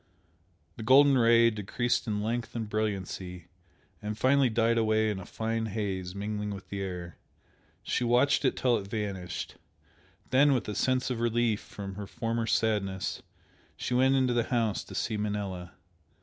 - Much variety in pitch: No, average, 3.0 semitones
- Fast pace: No, average, 165 wpm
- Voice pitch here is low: Yes, low, 110 Hz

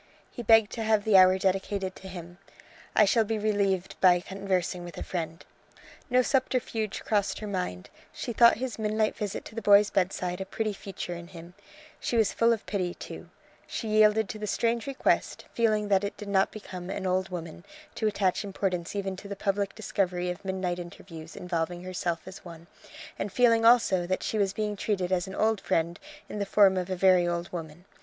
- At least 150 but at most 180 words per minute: No, average, 200 wpm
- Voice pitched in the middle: No, high, 195 Hz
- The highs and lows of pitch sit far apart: No, average, 3.1 semitones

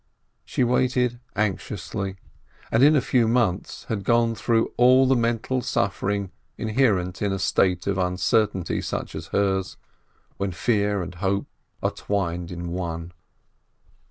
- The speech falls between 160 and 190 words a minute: No, average, 140 wpm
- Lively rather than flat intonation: No, average, 4.2 semitones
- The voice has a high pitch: No, low, 100 Hz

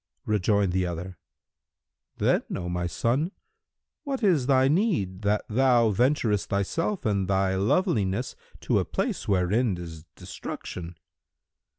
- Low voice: Yes, low, 105 Hz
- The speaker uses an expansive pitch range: Yes, wide, 6.1 semitones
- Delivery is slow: Yes, slow, 120 wpm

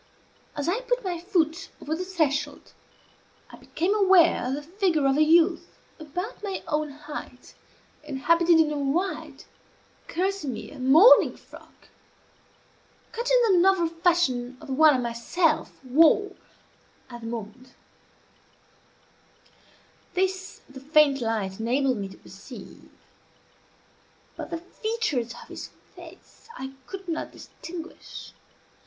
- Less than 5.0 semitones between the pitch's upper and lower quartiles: No, wide, 5.5 semitones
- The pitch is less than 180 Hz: No, very high, 315 Hz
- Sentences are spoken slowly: Yes, slow, 125 wpm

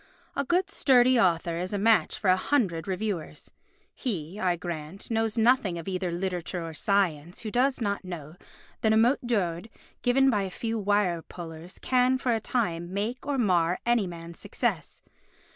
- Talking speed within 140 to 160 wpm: No, average, 175 wpm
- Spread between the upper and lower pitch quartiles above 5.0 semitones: Yes, wide, 5.4 semitones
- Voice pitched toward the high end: Yes, high, 200 Hz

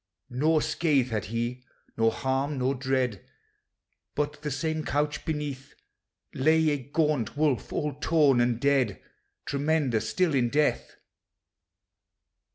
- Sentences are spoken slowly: Yes, slow, 120 wpm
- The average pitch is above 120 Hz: Yes, medium, 140 Hz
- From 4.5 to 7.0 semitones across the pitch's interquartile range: No, average, 3.2 semitones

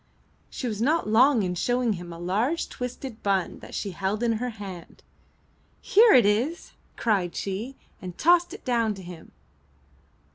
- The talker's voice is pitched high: Yes, high, 220 Hz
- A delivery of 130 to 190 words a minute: Yes, average, 160 wpm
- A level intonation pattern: No, average, 4.9 semitones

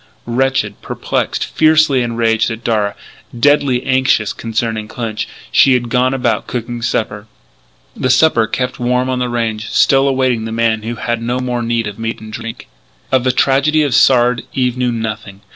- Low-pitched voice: Yes, low, 120 Hz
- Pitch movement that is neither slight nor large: No, narrow, 2.3 semitones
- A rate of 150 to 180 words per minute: Yes, average, 170 wpm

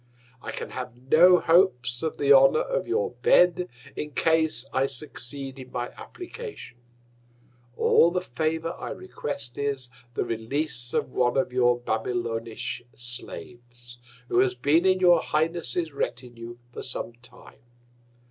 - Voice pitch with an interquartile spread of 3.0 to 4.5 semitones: No, average, 5.1 semitones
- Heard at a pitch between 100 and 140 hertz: Yes, low, 135 Hz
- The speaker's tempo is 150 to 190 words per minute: No, average, 140 wpm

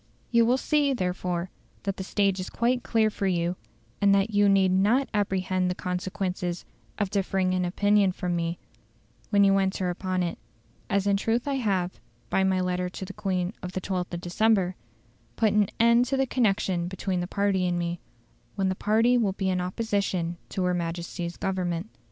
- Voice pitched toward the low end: No, high, 190 Hz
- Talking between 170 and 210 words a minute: Yes, average, 190 wpm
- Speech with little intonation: Yes, narrow, 2.3 semitones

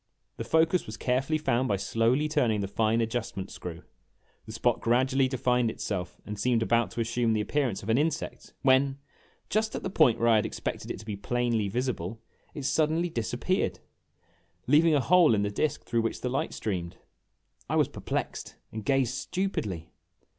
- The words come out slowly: No, average, 180 wpm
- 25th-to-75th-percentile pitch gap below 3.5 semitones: No, average, 4.2 semitones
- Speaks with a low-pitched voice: Yes, low, 120 Hz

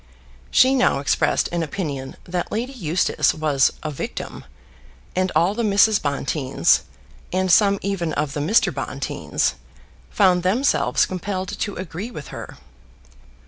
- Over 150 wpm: No, slow, 135 wpm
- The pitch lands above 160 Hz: Yes, medium, 185 Hz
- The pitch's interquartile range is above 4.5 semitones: Yes, average, 4.9 semitones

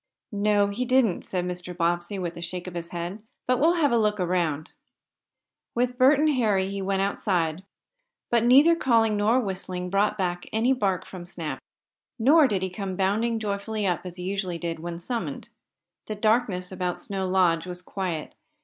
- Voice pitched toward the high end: Yes, high, 195 Hz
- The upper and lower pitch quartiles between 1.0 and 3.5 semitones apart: No, average, 3.9 semitones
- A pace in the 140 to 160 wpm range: No, average, 175 wpm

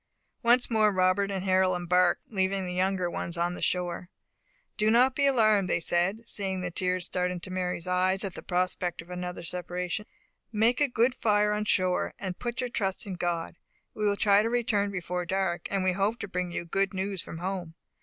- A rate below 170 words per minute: No, fast, 205 wpm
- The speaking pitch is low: No, high, 190 Hz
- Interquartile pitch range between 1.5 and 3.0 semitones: Yes, narrow, 2.6 semitones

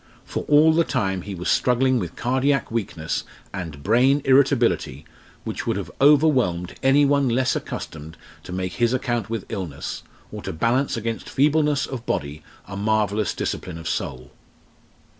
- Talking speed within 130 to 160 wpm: Yes, average, 155 wpm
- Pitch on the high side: No, low, 115 Hz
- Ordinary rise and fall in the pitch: No, wide, 6.7 semitones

